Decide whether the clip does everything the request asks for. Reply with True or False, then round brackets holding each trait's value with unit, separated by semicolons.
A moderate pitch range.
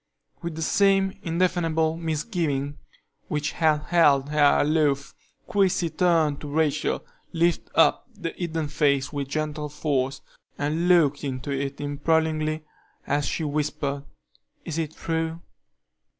False (2.3 semitones)